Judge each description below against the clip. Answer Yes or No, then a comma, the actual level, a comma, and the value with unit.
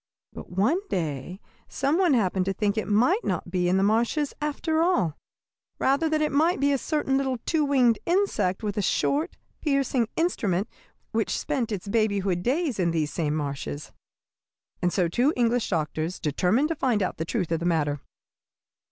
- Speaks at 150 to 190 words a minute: Yes, average, 180 wpm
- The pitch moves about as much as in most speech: No, wide, 8.0 semitones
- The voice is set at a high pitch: Yes, high, 220 Hz